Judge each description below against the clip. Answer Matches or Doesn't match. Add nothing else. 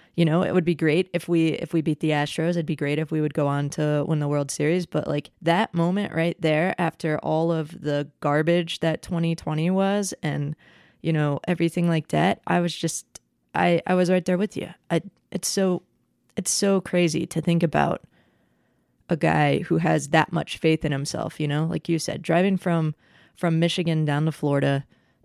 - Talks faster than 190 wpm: Matches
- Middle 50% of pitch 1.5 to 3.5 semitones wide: Matches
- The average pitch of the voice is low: Doesn't match